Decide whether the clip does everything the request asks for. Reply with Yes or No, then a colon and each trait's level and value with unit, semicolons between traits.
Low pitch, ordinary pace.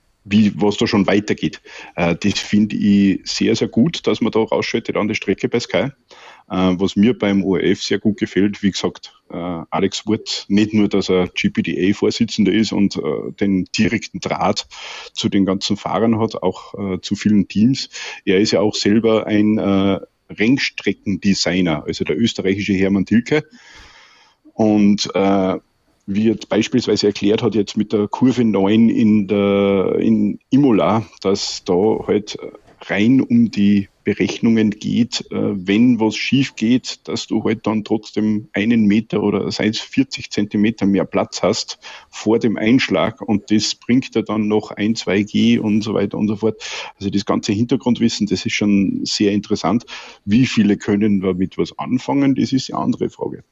Yes: low, 105 Hz; average, 165 wpm